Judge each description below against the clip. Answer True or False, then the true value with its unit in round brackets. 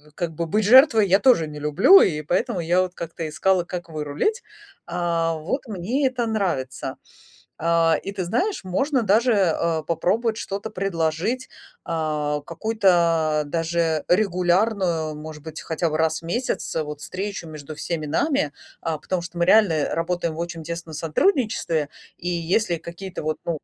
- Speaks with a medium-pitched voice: True (170 Hz)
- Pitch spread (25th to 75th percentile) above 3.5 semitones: True (3.9 semitones)